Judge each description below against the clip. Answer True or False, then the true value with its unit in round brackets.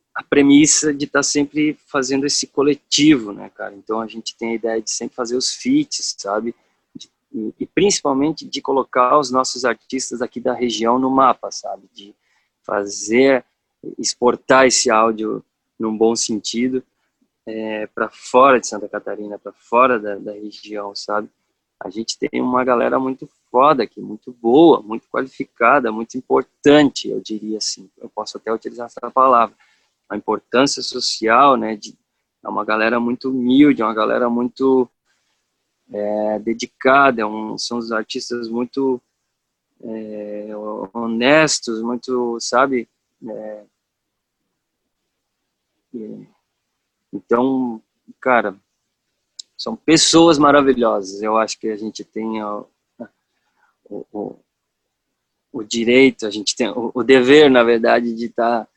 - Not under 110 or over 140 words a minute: True (135 wpm)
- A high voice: False (120 Hz)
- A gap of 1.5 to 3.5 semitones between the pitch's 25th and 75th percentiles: True (3.2 semitones)